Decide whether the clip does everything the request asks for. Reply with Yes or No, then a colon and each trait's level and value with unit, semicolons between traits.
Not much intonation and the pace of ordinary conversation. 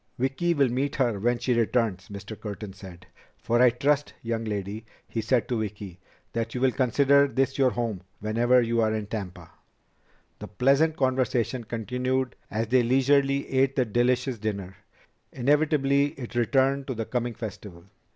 No: average, 3.5 semitones; average, 160 wpm